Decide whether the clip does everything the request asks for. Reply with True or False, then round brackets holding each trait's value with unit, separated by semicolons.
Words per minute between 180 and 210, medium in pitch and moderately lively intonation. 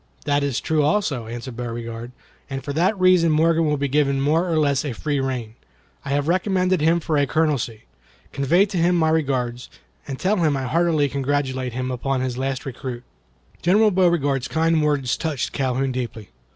True (185 wpm; 145 Hz; 4.0 semitones)